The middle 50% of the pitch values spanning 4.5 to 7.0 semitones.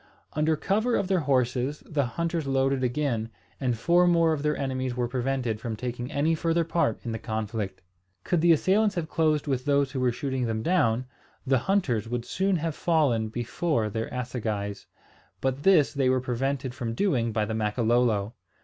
Yes: average, 5.1 semitones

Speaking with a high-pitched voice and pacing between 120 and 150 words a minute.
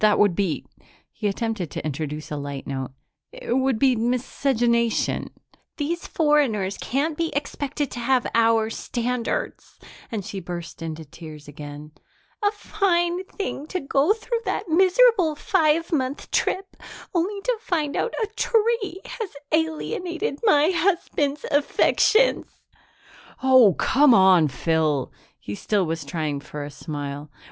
Yes: very high, 260 Hz; slow, 135 wpm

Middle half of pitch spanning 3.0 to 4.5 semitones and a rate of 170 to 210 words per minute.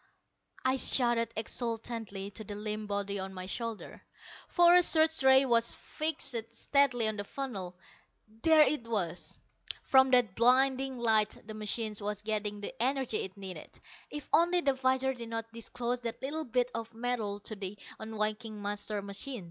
No: average, 4.0 semitones; average, 160 wpm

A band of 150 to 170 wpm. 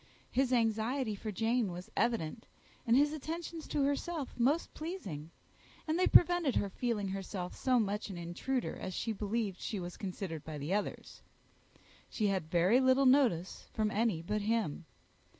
Yes: average, 160 wpm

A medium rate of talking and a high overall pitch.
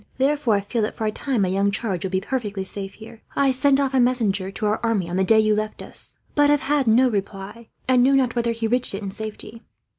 No: fast, 260 wpm; high, 220 Hz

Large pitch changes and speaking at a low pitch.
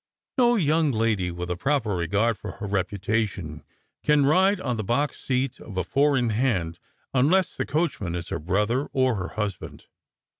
Yes: wide, 6.8 semitones; low, 115 Hz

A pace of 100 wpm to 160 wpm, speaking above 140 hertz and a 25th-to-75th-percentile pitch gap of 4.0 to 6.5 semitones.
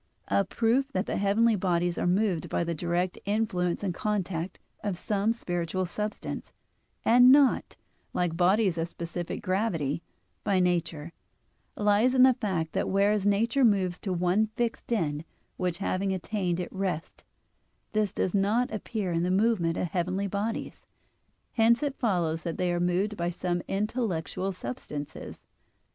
No: average, 150 wpm; high, 190 Hz; average, 3.4 semitones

